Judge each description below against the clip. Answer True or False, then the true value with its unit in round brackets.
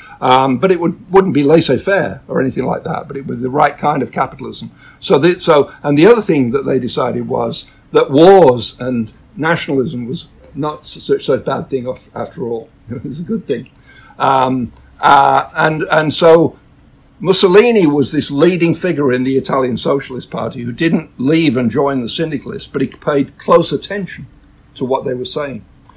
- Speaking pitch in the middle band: True (145 Hz)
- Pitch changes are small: False (4.8 semitones)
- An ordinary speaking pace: True (185 wpm)